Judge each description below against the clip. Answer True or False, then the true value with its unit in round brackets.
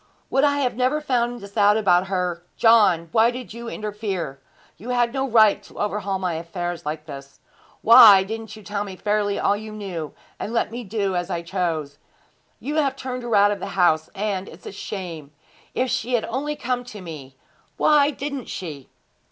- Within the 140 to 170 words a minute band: False (195 wpm)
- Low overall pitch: False (205 Hz)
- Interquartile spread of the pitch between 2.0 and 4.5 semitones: False (5.1 semitones)